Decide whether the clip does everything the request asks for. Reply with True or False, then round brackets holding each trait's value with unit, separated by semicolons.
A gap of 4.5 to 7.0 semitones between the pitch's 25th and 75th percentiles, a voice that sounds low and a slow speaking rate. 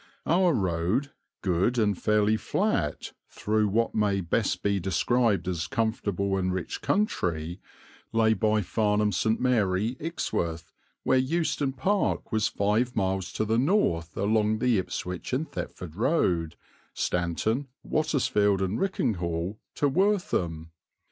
True (5.2 semitones; 105 Hz; 125 wpm)